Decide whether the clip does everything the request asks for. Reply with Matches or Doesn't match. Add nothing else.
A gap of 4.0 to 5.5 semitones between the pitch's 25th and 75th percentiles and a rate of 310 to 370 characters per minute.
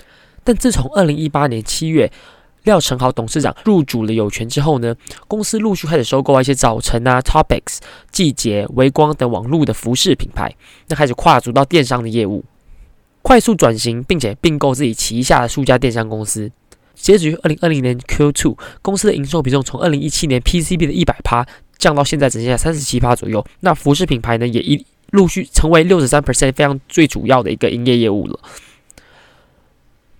Matches